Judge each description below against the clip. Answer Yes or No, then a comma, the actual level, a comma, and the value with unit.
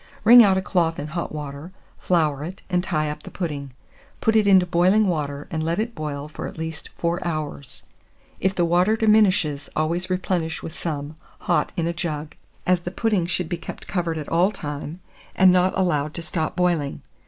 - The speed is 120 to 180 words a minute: No, average, 195 wpm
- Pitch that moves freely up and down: No, average, 3.2 semitones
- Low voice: No, medium, 170 Hz